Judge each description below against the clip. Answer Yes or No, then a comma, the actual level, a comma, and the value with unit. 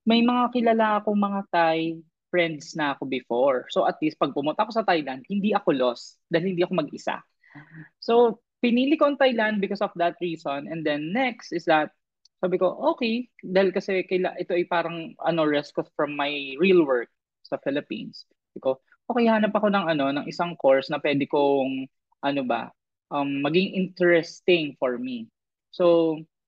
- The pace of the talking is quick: Yes, fast, 170 wpm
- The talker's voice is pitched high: No, medium, 175 Hz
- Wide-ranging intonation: Yes, wide, 5.8 semitones